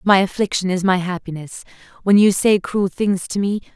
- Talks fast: No, average, 190 wpm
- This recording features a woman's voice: Yes, female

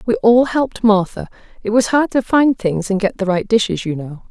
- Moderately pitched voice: No, high, 215 Hz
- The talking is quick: Yes, fast, 235 wpm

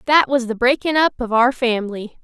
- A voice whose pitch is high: Yes, very high, 250 Hz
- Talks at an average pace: No, fast, 215 wpm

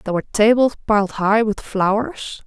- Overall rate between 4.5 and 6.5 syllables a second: Yes, 5.2 syllables/s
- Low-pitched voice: No, high, 215 Hz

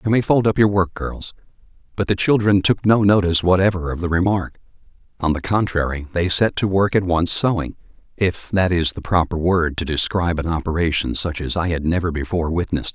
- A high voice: No, very low, 90 Hz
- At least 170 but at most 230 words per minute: Yes, average, 200 wpm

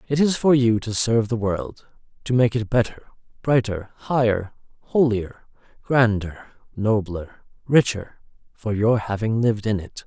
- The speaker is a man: Yes, male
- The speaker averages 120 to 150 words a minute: Yes, average, 145 wpm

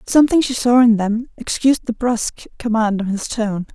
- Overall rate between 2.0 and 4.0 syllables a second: No, 5.6 syllables/s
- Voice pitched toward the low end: No, high, 230 Hz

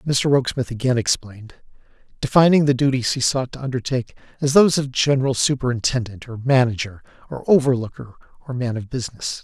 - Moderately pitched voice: No, low, 125 Hz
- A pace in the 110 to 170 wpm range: Yes, average, 155 wpm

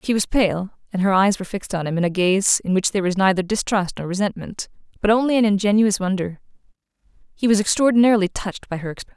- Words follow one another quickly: Yes, fast, 215 wpm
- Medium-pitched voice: No, high, 200 Hz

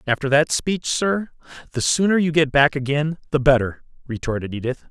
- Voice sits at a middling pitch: Yes, medium, 145 Hz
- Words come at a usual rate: Yes, average, 170 wpm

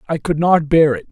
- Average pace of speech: No, fast, 270 wpm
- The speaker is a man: Yes, male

